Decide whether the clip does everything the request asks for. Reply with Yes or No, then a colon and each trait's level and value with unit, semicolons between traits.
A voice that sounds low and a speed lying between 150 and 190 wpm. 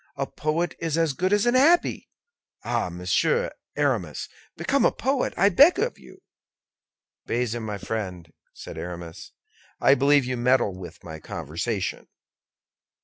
No: low, 130 Hz; average, 140 wpm